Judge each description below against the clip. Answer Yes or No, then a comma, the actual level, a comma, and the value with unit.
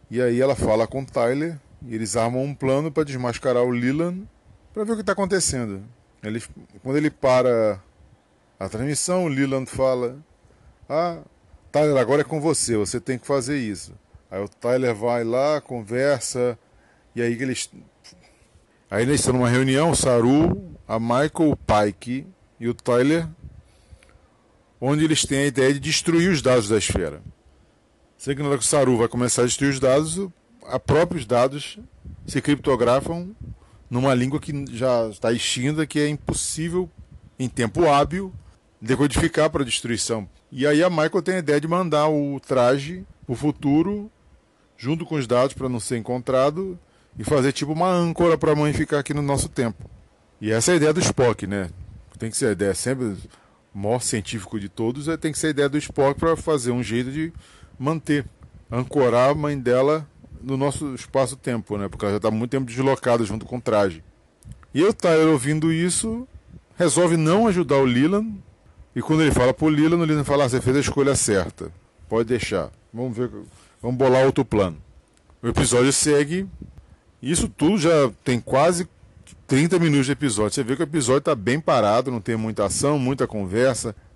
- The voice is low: Yes, low, 130 Hz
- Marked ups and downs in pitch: No, average, 4.6 semitones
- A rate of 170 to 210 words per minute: Yes, average, 175 wpm